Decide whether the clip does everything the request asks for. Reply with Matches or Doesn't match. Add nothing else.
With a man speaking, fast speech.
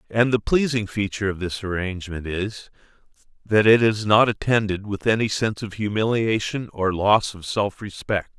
Doesn't match